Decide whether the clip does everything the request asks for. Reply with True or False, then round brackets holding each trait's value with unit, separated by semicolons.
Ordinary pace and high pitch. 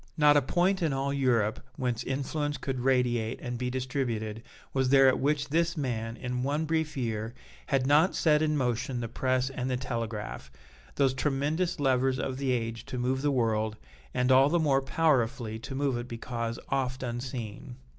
False (180 wpm; 130 Hz)